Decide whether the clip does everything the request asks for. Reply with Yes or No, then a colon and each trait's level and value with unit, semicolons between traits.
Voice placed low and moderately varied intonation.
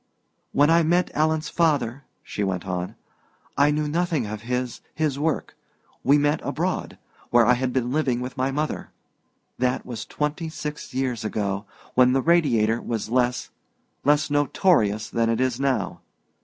Yes: low, 130 Hz; average, 4.2 semitones